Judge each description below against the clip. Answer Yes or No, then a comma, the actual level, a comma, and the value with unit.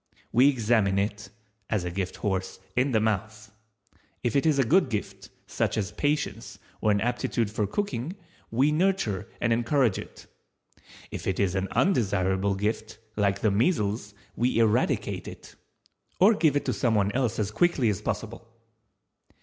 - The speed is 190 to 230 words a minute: No, average, 155 wpm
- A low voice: Yes, low, 110 Hz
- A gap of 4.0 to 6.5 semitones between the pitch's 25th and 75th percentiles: Yes, average, 4.4 semitones